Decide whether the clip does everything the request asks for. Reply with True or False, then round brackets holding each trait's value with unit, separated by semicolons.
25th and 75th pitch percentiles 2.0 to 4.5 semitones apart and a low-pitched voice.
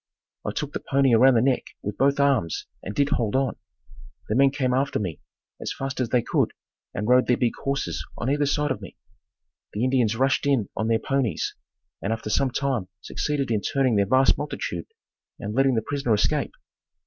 True (3.6 semitones; 130 Hz)